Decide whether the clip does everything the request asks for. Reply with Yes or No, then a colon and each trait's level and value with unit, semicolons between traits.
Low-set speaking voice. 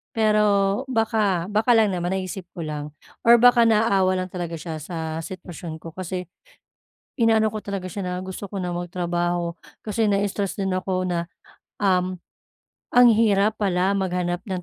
No: high, 190 Hz